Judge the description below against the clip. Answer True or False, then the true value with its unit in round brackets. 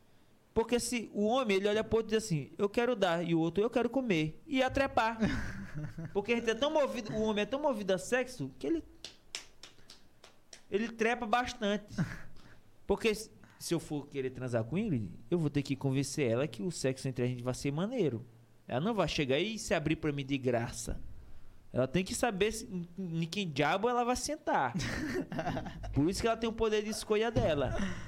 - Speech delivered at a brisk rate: True (210 wpm)